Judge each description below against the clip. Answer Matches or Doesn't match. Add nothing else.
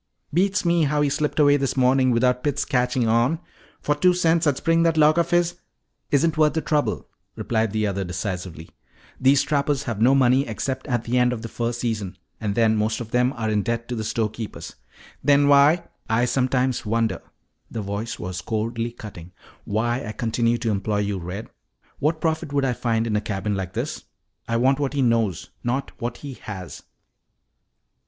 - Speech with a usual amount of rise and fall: Matches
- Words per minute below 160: Doesn't match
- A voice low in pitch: Matches